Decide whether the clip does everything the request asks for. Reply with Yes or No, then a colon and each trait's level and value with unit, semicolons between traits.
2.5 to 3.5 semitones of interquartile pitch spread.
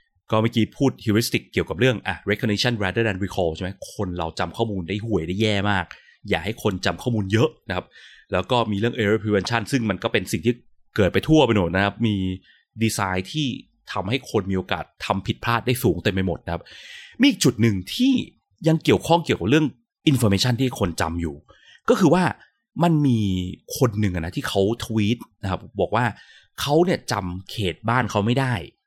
No: average, 4.2 semitones